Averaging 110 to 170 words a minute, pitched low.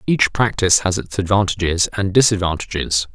Yes: slow, 135 wpm; very low, 95 Hz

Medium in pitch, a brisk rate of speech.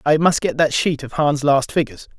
Yes: medium, 145 Hz; fast, 245 wpm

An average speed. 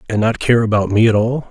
No: fast, 280 wpm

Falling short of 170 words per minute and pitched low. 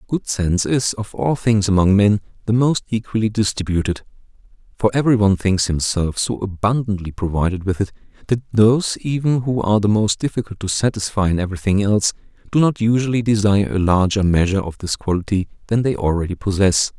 No: average, 175 wpm; low, 105 Hz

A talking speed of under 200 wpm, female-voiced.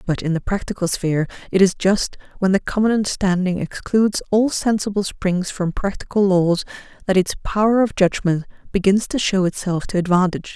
Yes: average, 170 wpm; female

